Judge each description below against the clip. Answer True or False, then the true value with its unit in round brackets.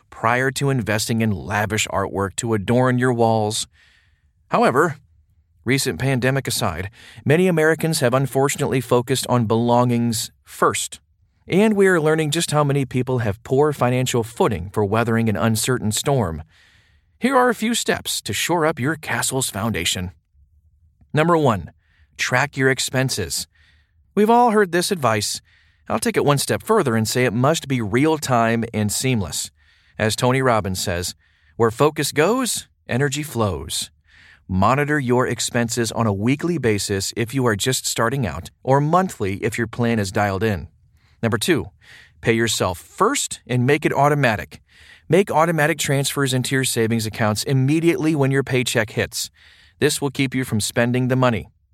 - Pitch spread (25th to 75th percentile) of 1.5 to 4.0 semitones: False (4.9 semitones)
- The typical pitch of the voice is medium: False (120 Hz)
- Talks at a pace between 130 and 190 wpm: True (155 wpm)